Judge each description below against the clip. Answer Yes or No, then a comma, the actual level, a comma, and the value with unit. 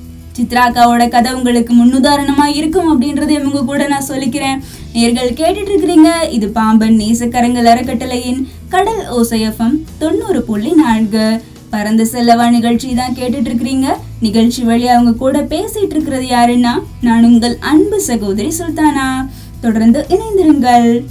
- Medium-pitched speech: No, high, 245 Hz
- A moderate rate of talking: Yes, average, 120 wpm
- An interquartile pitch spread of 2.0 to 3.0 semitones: No, average, 3.7 semitones